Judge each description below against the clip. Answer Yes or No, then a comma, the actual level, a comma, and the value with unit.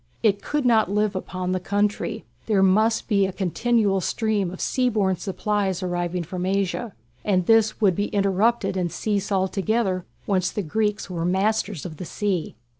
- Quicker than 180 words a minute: No, average, 170 wpm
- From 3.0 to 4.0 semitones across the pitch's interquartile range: No, narrow, 2.6 semitones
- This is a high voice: Yes, high, 195 Hz